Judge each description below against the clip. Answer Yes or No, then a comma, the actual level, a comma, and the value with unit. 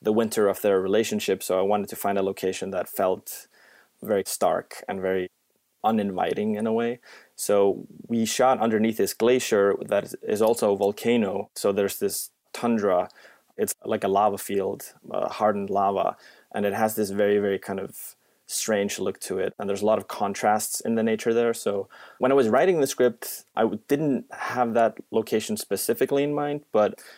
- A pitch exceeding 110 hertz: No, low, 105 Hz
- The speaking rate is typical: Yes, average, 185 wpm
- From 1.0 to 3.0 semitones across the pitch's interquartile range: Yes, average, 2.7 semitones